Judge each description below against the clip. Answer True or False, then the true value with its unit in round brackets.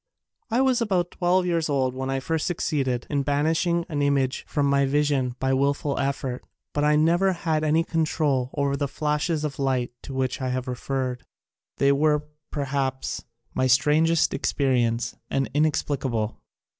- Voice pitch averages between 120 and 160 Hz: True (140 Hz)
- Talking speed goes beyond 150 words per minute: True (165 wpm)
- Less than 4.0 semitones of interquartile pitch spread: True (2.9 semitones)